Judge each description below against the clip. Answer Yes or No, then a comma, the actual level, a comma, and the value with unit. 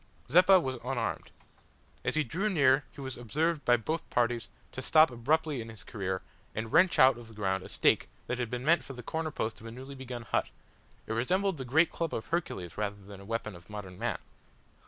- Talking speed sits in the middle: No, fast, 220 wpm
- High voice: No, low, 125 Hz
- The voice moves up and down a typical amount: No, wide, 5.7 semitones